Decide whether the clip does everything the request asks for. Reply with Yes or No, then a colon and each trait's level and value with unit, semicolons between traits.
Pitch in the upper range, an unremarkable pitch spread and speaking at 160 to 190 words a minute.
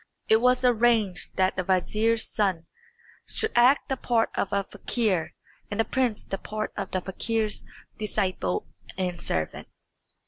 No: high, 215 Hz; average, 3.7 semitones; average, 145 wpm